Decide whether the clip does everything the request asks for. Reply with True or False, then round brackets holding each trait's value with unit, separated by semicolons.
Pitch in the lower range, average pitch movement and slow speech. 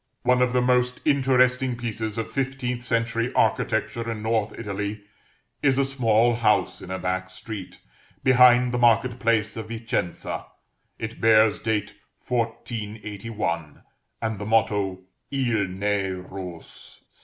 True (115 Hz; 3.2 semitones; 130 wpm)